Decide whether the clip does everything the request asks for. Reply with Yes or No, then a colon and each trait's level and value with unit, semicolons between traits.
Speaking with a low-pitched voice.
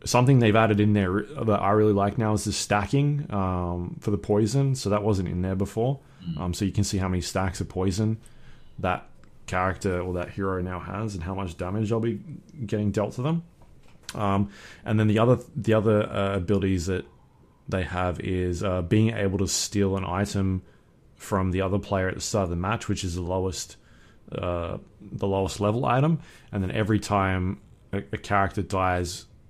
Yes: low, 100 Hz